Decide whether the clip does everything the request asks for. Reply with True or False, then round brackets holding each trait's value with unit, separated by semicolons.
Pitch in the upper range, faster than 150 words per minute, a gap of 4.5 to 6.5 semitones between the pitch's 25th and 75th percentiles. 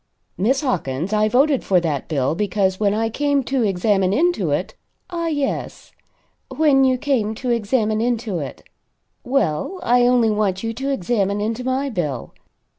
True (225 Hz; 170 wpm; 5.3 semitones)